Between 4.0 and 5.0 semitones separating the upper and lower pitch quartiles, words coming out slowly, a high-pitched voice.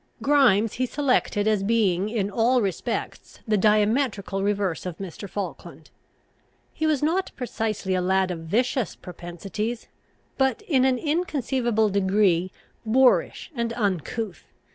Yes: average, 4.6 semitones; slow, 125 wpm; high, 215 Hz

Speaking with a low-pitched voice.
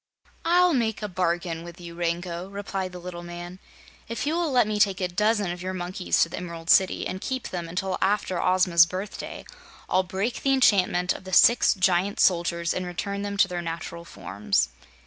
No: medium, 185 Hz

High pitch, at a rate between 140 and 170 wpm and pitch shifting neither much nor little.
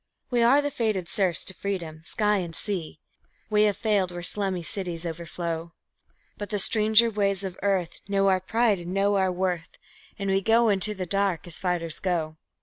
No: high, 195 Hz; average, 185 wpm; average, 3.0 semitones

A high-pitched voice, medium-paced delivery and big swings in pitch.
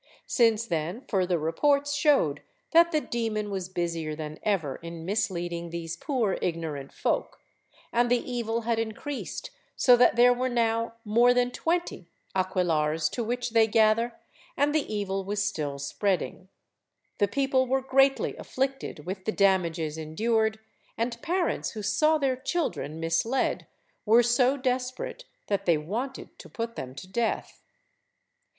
Yes: high, 220 Hz; average, 145 wpm; wide, 6.4 semitones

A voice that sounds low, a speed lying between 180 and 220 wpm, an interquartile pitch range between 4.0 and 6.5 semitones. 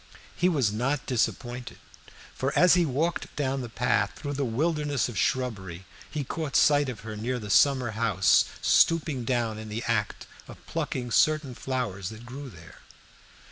No: low, 125 Hz; average, 165 wpm; average, 4.4 semitones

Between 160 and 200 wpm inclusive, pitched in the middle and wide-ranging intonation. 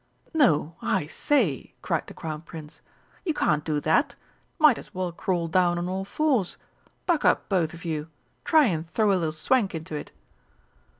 Yes: average, 175 wpm; medium, 175 Hz; wide, 5.7 semitones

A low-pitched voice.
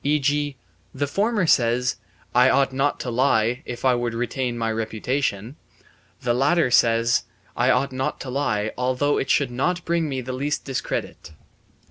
Yes: low, 130 Hz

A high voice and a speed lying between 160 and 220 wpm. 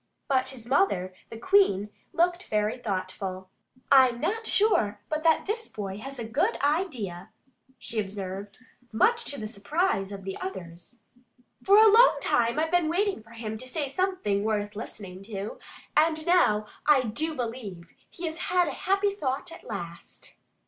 Yes: very high, 250 Hz; average, 165 wpm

